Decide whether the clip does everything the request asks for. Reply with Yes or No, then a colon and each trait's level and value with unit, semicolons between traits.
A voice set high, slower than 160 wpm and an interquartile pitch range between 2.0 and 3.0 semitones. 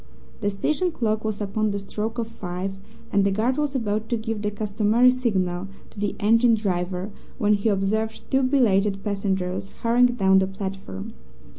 No: high, 210 Hz; average, 170 wpm; average, 2.7 semitones